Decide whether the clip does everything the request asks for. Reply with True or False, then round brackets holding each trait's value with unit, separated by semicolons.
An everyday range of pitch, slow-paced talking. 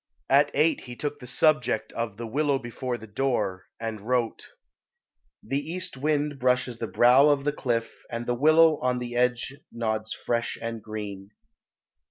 False (3.7 semitones; 165 wpm)